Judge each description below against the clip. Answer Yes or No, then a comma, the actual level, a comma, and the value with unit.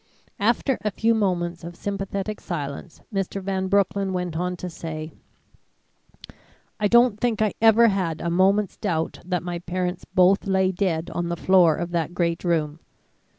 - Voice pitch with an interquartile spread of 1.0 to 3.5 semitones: Yes, average, 2.7 semitones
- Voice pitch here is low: No, medium, 185 Hz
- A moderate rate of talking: Yes, average, 160 wpm